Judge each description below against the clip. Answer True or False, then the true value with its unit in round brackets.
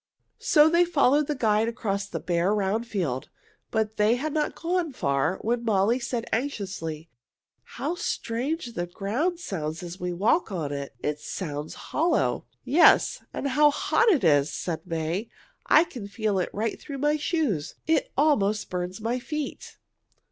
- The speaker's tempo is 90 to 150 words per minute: False (160 wpm)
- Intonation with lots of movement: True (8.5 semitones)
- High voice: True (220 Hz)